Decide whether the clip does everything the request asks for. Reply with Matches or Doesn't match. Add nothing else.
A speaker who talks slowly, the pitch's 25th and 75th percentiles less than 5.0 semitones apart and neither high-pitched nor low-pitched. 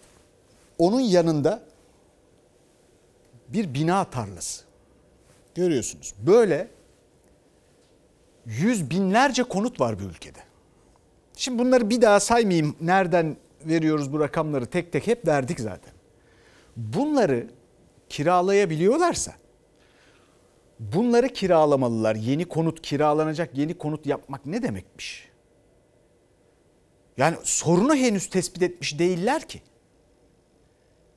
Doesn't match